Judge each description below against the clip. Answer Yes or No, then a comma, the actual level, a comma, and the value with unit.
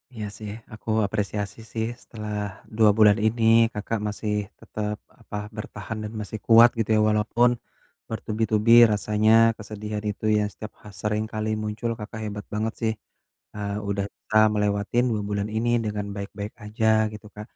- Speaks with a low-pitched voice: Yes, low, 105 Hz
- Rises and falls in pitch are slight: Yes, narrow, 1.1 semitones